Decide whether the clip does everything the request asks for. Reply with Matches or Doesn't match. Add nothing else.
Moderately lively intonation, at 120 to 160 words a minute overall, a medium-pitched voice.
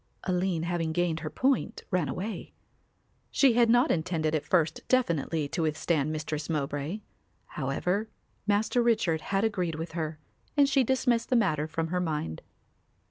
Doesn't match